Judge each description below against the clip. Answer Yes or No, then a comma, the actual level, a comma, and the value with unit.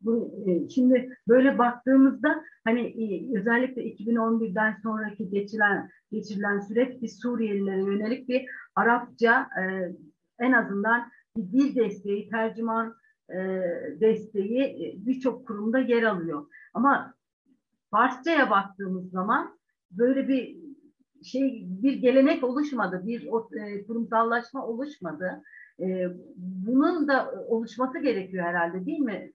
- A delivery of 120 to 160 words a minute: No, slow, 95 wpm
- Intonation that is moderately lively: Yes, average, 4.2 semitones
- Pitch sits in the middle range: No, high, 230 Hz